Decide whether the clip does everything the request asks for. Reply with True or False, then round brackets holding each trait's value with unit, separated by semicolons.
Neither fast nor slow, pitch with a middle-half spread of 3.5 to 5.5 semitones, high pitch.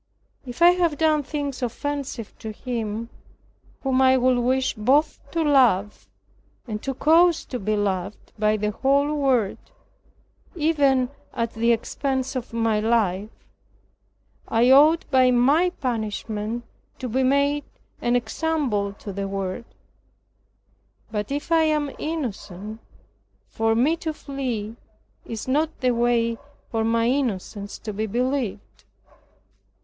False (130 wpm; 4.5 semitones; 245 Hz)